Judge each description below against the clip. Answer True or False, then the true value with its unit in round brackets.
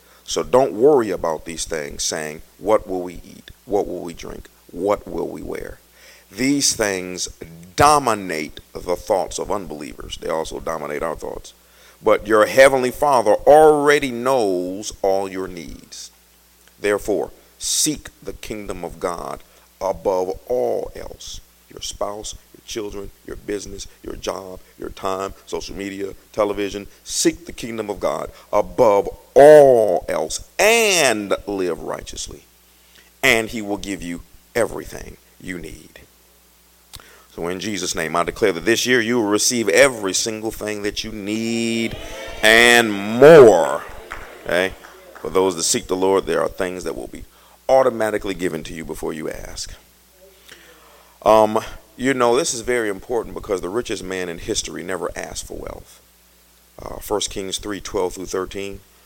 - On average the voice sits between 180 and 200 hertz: False (100 Hz)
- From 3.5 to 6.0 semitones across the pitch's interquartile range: True (4.6 semitones)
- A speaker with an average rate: True (150 wpm)